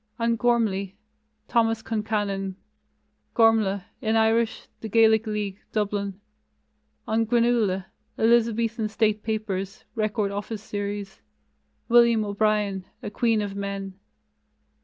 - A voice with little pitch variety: Yes, narrow, 2.0 semitones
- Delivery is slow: Yes, slow, 100 wpm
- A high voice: Yes, high, 215 Hz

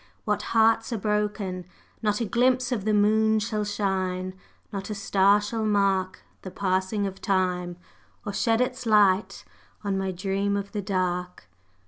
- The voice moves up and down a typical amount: No, narrow, 2.3 semitones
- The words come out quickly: No, average, 155 wpm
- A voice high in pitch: Yes, high, 200 Hz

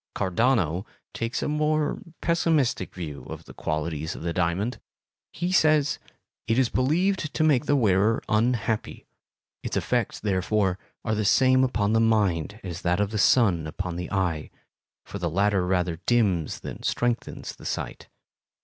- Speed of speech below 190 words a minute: Yes, average, 155 wpm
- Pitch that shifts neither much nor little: No, wide, 6.2 semitones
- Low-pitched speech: Yes, low, 105 Hz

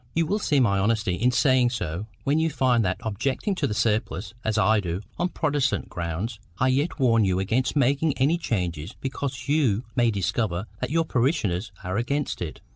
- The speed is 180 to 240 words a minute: Yes, average, 190 wpm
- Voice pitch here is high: No, low, 120 Hz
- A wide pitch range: Yes, wide, 5.9 semitones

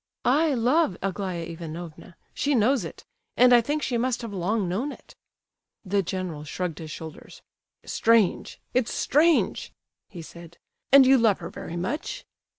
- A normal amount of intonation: No, wide, 6.9 semitones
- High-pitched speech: Yes, high, 205 Hz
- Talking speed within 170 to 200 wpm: No, average, 140 wpm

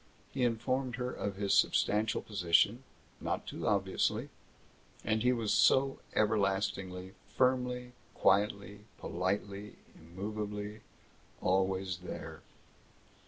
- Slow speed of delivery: Yes, slow, 95 wpm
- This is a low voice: Yes, low, 105 Hz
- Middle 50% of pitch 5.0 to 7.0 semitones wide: No, average, 3.6 semitones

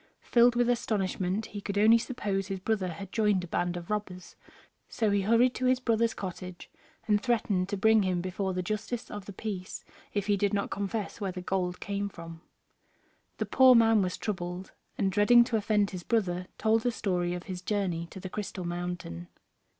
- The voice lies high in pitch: Yes, high, 200 Hz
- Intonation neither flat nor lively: Yes, average, 3.3 semitones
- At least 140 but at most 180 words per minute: No, average, 195 wpm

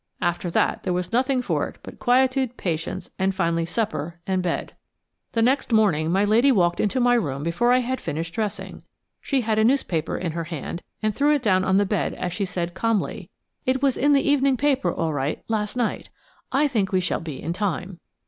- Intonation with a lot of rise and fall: Yes, wide, 6.3 semitones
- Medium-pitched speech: No, high, 205 Hz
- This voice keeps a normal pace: No, fast, 210 wpm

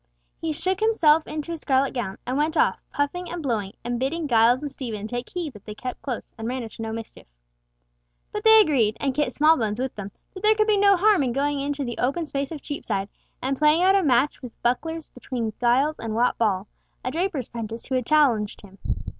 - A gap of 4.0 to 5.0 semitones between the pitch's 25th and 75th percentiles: No, wide, 5.4 semitones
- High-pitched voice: Yes, very high, 270 Hz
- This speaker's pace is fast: Yes, fast, 220 wpm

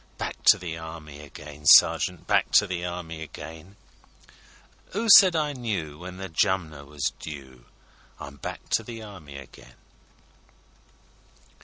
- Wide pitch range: No, average, 4.3 semitones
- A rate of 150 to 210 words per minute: No, average, 140 wpm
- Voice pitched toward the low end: Yes, very low, 80 Hz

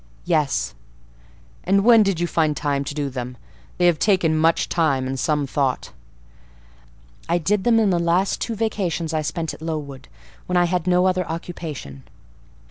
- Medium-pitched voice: Yes, medium, 165 Hz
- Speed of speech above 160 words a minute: Yes, average, 170 wpm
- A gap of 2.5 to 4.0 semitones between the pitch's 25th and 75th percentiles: Yes, average, 3.7 semitones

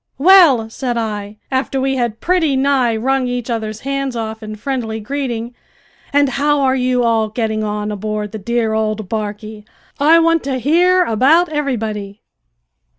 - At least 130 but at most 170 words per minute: Yes, average, 155 wpm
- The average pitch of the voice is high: Yes, high, 240 Hz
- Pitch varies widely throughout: No, average, 4.0 semitones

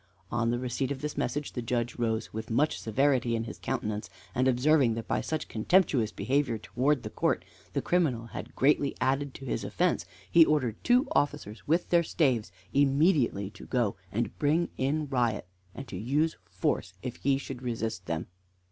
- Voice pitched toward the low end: Yes, low, 125 Hz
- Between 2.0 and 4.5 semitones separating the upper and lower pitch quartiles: Yes, average, 4.2 semitones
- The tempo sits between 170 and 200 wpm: Yes, average, 180 wpm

